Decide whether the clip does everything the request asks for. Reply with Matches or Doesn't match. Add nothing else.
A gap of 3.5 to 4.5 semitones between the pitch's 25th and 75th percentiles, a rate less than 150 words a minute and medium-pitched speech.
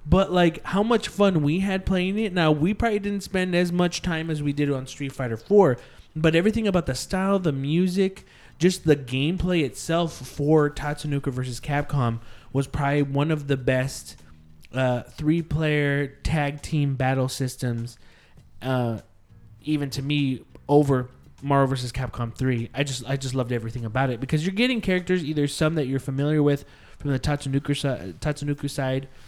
Doesn't match